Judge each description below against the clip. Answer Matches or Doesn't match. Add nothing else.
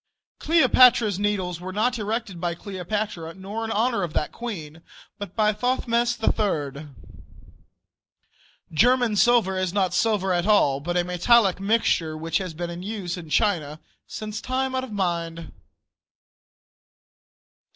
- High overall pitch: Matches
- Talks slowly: Matches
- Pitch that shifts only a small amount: Doesn't match